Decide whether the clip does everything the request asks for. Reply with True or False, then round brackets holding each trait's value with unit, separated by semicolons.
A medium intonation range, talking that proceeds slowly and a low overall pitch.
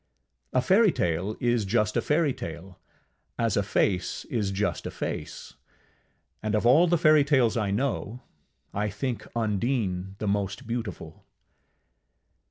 True (4.2 semitones; 120 wpm; 110 Hz)